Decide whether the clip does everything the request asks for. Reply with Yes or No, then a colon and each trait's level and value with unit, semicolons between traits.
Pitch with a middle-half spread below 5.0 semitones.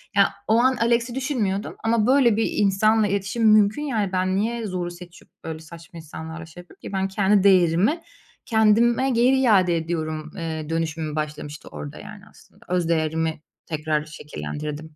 No: wide, 5.5 semitones